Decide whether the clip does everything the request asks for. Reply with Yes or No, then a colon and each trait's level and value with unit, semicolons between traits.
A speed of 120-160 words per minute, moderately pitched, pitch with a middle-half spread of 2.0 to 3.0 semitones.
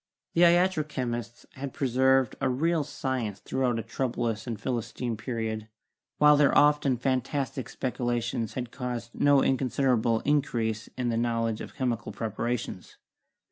No: average, 140 wpm; low, 125 Hz; average, 2.7 semitones